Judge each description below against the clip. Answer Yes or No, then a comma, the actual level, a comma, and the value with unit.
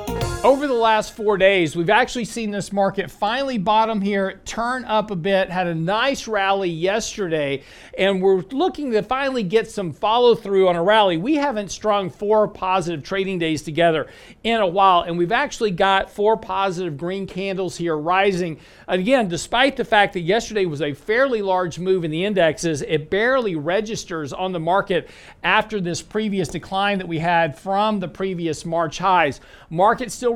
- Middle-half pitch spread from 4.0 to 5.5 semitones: No, average, 3.6 semitones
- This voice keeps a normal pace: Yes, average, 175 wpm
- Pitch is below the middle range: No, high, 195 Hz